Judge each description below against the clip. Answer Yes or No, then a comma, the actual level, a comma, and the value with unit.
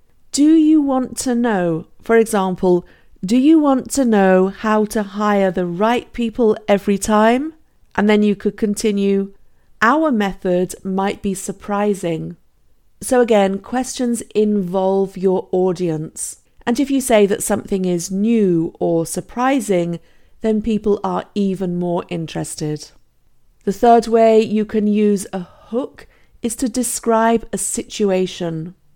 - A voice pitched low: No, high, 205 Hz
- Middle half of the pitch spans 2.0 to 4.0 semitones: Yes, average, 3.6 semitones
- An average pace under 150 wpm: Yes, slow, 135 wpm